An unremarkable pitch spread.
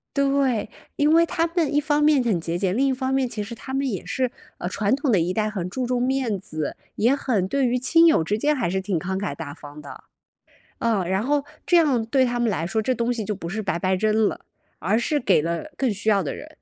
No: wide, 6.0 semitones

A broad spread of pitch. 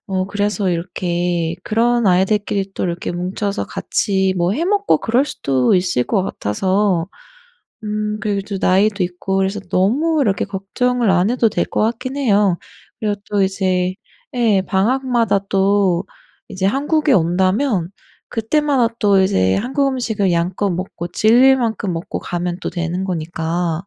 No: average, 3.9 semitones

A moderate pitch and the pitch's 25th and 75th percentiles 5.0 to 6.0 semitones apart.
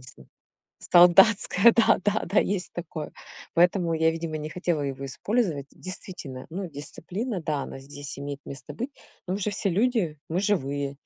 Yes: medium, 170 Hz; wide, 5.4 semitones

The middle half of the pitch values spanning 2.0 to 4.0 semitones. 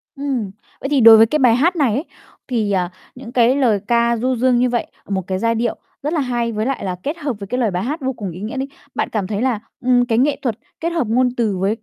Yes: average, 3.4 semitones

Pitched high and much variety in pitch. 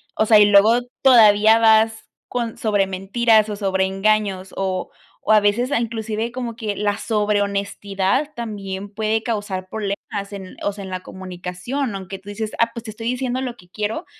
No: high, 210 Hz; narrow, 2.5 semitones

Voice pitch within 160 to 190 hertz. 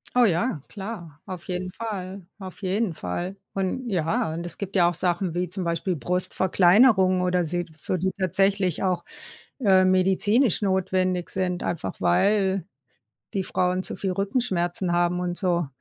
Yes: medium, 185 Hz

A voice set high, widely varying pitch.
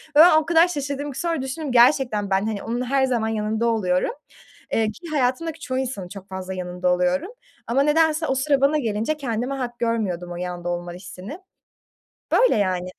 Yes: high, 240 Hz; wide, 6.9 semitones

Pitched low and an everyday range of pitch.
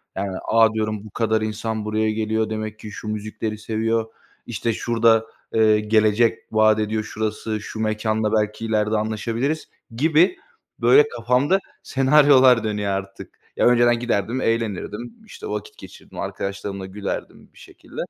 No: low, 110 Hz; narrow, 1.3 semitones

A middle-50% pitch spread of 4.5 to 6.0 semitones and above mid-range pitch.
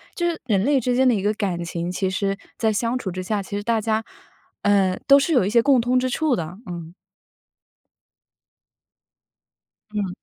Yes: average, 4.9 semitones; high, 210 Hz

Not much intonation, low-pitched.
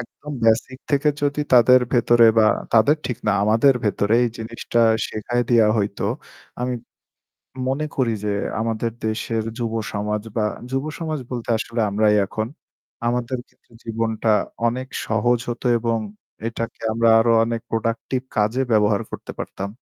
Yes: narrow, 2.0 semitones; low, 115 Hz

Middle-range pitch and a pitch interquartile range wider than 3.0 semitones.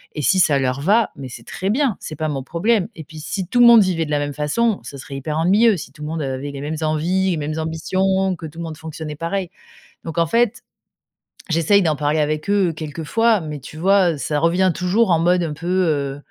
Yes: medium, 165 Hz; average, 4.0 semitones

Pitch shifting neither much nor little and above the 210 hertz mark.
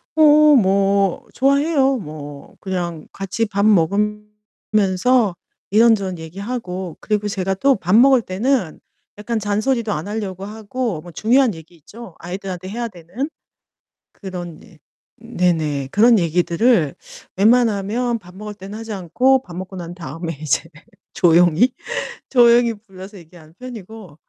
No: average, 4.5 semitones; high, 200 Hz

